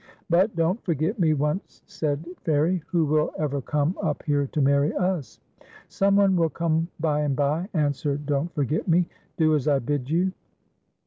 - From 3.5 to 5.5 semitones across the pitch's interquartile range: No, average, 2.8 semitones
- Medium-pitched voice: Yes, medium, 155 Hz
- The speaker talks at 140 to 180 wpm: No, average, 195 wpm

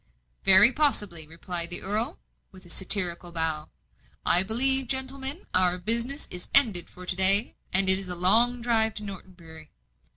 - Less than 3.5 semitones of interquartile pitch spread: No, average, 5.0 semitones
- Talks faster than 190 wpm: No, average, 165 wpm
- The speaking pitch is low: No, high, 190 Hz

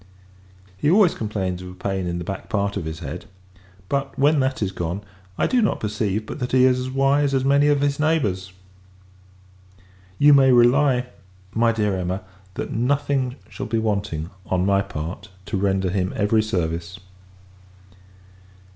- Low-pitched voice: Yes, low, 110 Hz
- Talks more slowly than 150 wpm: No, average, 165 wpm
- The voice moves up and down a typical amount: No, wide, 6.2 semitones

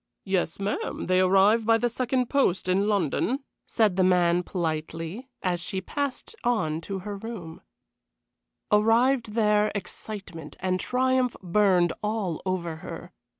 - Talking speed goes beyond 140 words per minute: No, slow, 135 wpm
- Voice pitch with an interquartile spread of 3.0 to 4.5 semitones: Yes, average, 4.1 semitones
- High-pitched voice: Yes, high, 195 Hz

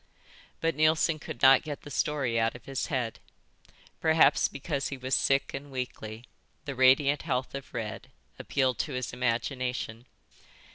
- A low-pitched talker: Yes, low, 130 Hz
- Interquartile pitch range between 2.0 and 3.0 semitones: Yes, narrow, 2.6 semitones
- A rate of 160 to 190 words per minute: No, average, 150 wpm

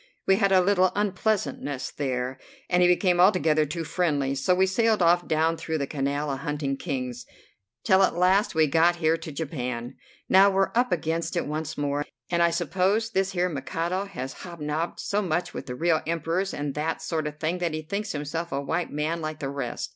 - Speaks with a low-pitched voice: No, medium, 165 Hz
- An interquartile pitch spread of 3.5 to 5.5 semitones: Yes, average, 3.8 semitones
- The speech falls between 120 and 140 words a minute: No, average, 200 wpm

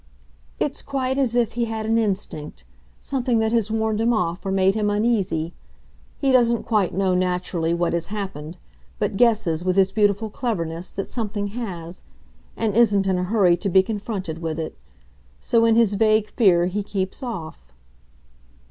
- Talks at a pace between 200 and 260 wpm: No, average, 170 wpm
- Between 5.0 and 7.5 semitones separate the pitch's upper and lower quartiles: No, average, 3.9 semitones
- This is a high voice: Yes, high, 205 Hz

